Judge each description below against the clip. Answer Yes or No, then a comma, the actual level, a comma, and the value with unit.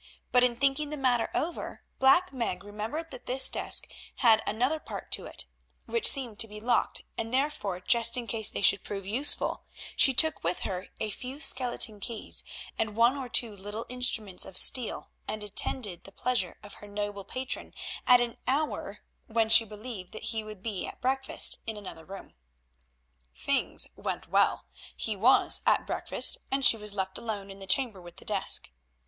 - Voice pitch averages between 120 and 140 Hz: No, high, 225 Hz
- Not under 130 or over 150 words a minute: No, average, 180 wpm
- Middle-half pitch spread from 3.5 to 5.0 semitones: Yes, average, 3.9 semitones